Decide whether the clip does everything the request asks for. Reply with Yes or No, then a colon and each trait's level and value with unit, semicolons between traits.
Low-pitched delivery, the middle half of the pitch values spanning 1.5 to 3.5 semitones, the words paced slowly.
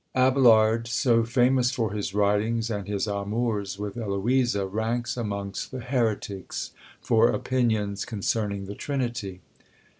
Yes: low, 110 Hz; average, 3.1 semitones; slow, 120 wpm